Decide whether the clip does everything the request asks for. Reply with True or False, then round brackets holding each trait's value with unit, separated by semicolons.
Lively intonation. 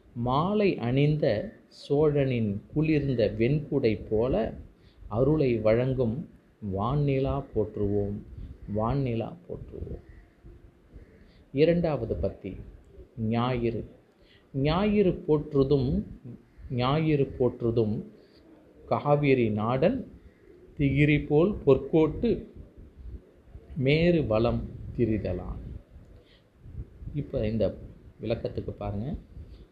True (5.8 semitones)